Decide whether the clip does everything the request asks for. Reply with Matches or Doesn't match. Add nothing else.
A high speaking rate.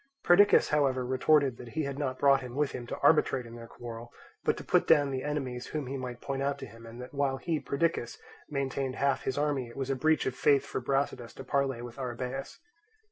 Matches